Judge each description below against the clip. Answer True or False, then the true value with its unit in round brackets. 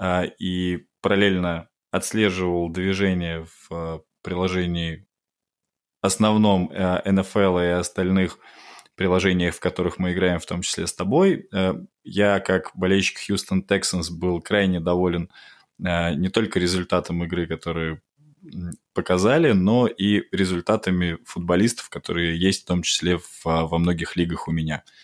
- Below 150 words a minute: True (115 wpm)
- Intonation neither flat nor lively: False (1.8 semitones)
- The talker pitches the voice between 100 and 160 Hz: False (90 Hz)